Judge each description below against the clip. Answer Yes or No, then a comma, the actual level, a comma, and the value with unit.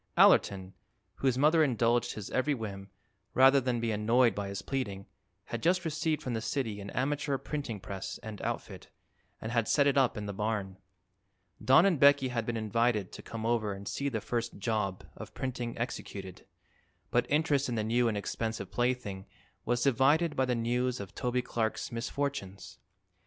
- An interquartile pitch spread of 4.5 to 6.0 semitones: No, average, 4.1 semitones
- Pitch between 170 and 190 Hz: No, low, 120 Hz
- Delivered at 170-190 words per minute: Yes, average, 175 wpm